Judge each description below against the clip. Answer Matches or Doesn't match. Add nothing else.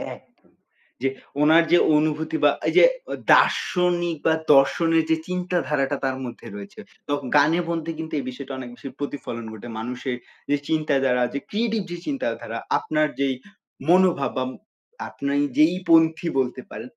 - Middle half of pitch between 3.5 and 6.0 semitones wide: Matches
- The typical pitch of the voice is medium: Matches